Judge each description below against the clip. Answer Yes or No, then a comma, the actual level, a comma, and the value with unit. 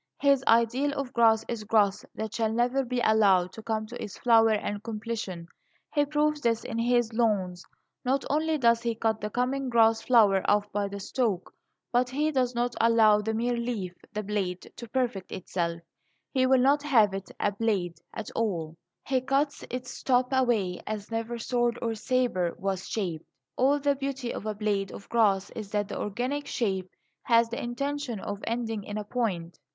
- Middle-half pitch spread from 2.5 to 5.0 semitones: Yes, average, 3.4 semitones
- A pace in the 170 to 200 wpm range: Yes, average, 185 wpm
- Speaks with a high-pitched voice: Yes, high, 230 Hz